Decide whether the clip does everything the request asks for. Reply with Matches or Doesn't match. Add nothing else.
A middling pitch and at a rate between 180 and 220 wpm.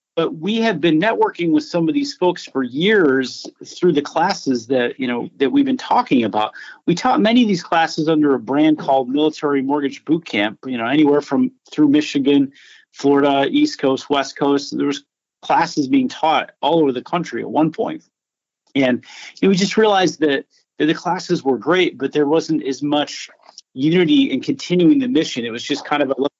Matches